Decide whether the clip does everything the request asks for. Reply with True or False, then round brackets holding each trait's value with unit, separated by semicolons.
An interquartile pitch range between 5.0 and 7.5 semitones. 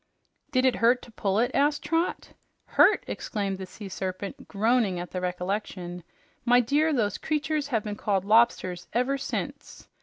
True (5.3 semitones)